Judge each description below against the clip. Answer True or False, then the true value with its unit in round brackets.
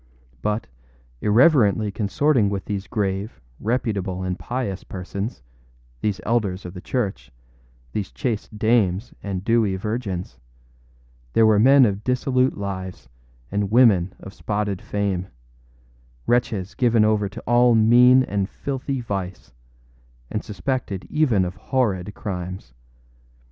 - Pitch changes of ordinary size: True (3.9 semitones)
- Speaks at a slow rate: True (120 wpm)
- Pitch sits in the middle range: False (105 Hz)